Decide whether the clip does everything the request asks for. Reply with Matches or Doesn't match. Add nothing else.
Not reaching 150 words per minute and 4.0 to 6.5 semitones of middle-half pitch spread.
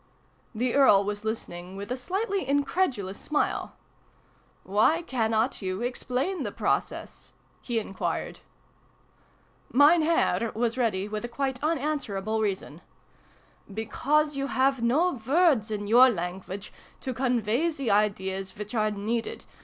Matches